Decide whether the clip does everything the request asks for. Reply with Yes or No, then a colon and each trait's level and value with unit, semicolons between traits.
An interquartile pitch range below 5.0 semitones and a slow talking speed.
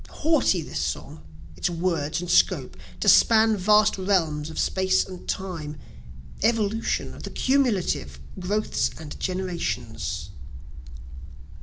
No: average, 5.3 semitones; slow, 110 wpm